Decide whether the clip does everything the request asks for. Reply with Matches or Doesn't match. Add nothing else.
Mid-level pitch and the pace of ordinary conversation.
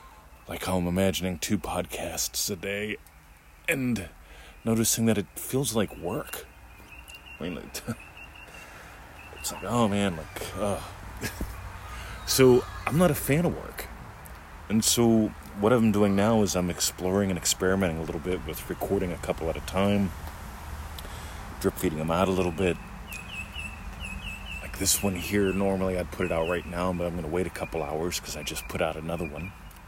Doesn't match